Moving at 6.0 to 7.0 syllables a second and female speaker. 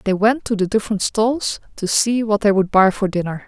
No: 5.2 syllables/s; female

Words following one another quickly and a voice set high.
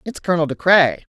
No: fast, 210 wpm; medium, 165 Hz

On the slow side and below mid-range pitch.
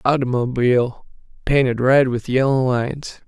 Yes: slow, 110 wpm; low, 130 Hz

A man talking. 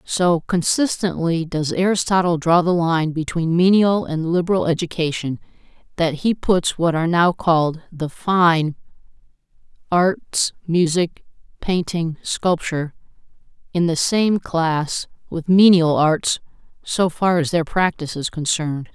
No: female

